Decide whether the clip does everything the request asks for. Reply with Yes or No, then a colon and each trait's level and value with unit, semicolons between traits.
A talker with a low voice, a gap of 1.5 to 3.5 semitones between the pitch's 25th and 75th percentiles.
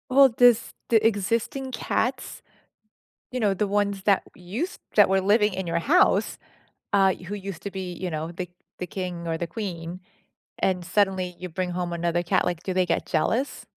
No: high, 190 Hz; average, 3.1 semitones